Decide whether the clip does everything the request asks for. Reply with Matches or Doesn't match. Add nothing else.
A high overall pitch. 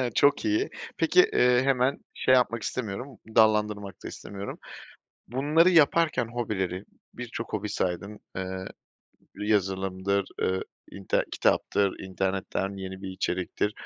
Doesn't match